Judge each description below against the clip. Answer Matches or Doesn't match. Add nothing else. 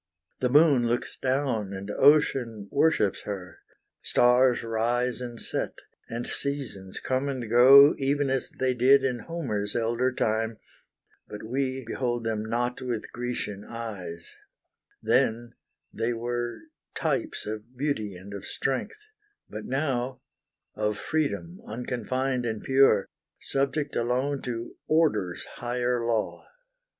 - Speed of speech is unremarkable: Doesn't match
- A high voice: Doesn't match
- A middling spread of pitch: Matches